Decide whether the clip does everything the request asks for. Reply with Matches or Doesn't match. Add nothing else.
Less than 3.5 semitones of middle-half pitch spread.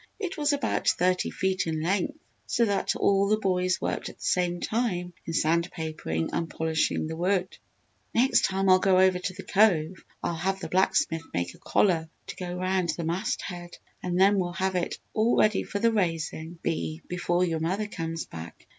Matches